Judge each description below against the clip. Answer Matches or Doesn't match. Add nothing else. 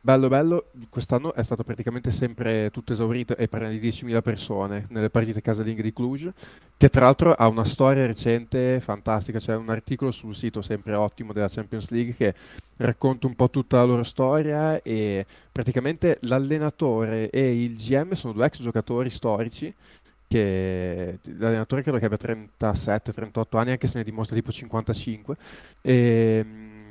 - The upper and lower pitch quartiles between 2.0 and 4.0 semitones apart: Matches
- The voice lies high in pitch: Doesn't match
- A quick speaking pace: Doesn't match